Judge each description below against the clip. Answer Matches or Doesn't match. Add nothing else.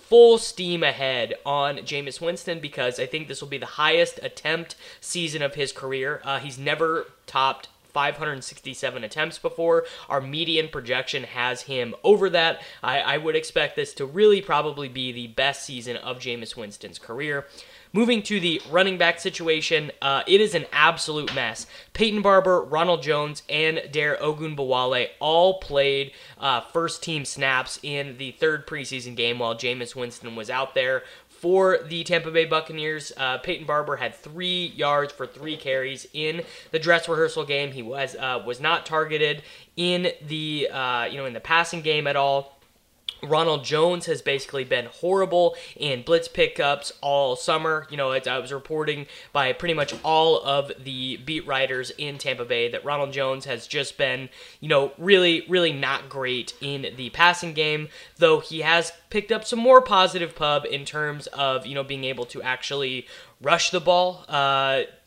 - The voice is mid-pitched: Matches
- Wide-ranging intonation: Doesn't match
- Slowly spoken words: Doesn't match